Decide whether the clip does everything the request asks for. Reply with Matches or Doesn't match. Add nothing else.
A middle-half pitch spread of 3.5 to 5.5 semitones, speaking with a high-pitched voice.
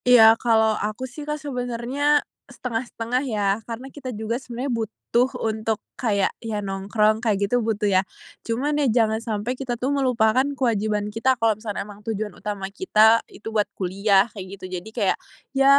Doesn't match